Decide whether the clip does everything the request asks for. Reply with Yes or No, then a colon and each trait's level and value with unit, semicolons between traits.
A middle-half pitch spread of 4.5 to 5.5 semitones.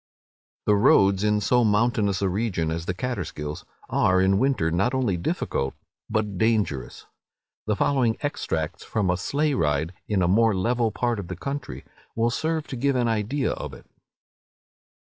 Yes: average, 5.0 semitones